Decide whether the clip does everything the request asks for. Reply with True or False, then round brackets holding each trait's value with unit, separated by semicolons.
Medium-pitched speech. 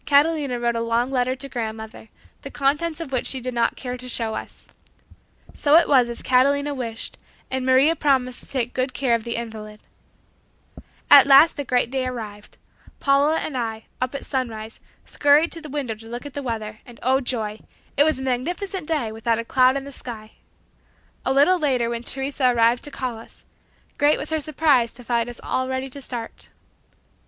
False (255 Hz)